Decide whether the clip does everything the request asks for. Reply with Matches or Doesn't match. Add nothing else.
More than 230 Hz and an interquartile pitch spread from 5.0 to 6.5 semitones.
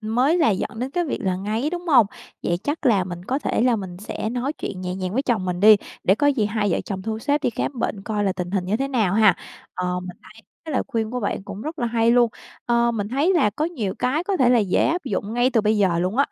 Doesn't match